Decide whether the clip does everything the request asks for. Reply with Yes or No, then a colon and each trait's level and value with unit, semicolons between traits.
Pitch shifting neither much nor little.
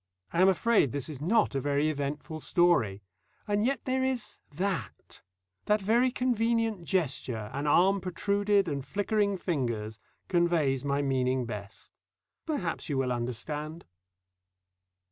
No: wide, 7.2 semitones